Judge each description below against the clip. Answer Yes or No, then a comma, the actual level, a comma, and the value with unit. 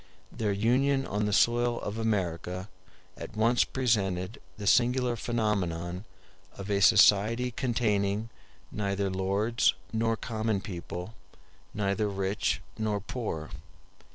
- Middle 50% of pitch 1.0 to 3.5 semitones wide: Yes, average, 2.9 semitones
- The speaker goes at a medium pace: No, slow, 110 wpm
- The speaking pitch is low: Yes, low, 105 Hz